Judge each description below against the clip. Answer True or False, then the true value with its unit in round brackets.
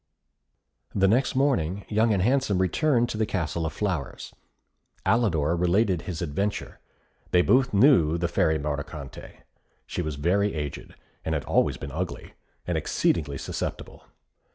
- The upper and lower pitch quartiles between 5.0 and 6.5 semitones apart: True (5.5 semitones)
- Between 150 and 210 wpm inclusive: False (135 wpm)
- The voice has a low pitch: True (90 Hz)